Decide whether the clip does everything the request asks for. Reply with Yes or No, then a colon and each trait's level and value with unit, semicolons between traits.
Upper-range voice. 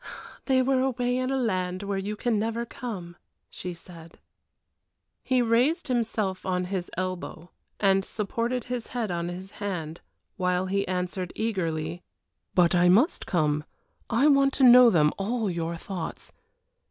Yes: high, 195 Hz